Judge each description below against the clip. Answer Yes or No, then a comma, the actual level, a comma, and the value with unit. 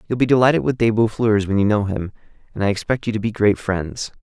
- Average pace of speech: No, fast, 255 wpm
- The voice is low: Yes, low, 105 Hz